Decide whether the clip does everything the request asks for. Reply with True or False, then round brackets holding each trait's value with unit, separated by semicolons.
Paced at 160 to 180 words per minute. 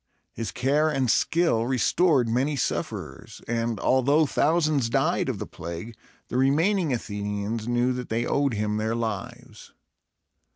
False (135 wpm)